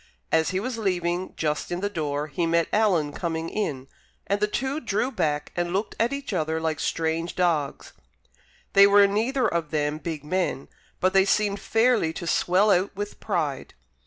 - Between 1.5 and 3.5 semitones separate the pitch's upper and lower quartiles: No, average, 4.3 semitones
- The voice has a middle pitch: Yes, medium, 180 Hz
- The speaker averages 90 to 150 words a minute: No, average, 180 wpm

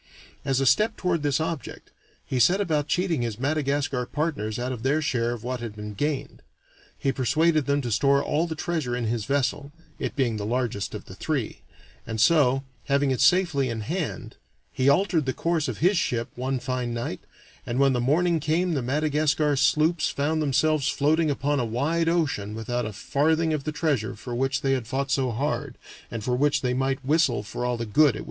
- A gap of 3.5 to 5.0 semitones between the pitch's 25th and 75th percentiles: Yes, average, 4.0 semitones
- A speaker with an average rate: No, fast, 210 wpm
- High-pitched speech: No, medium, 140 Hz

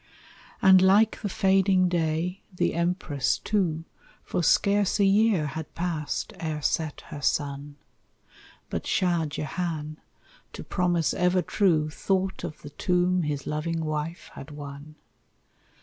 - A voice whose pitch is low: No, medium, 170 Hz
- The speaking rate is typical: No, slow, 130 wpm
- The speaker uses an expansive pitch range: No, average, 3.4 semitones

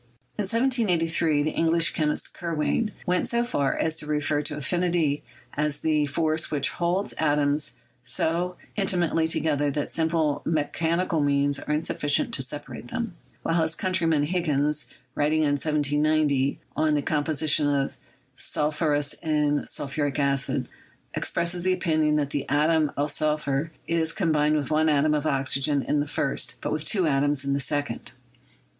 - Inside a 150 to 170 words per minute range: Yes, average, 160 wpm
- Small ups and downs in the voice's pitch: Yes, narrow, 2.3 semitones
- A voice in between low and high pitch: Yes, medium, 150 Hz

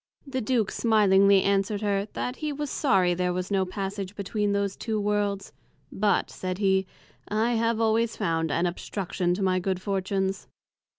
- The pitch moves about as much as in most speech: No, narrow, 2.2 semitones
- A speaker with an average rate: Yes, average, 165 wpm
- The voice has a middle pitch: No, high, 200 Hz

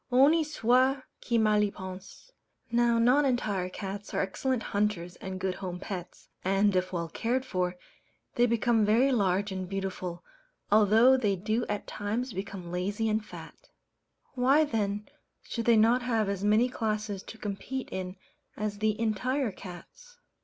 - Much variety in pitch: No, average, 3.9 semitones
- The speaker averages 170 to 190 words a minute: No, average, 155 wpm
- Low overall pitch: No, high, 210 Hz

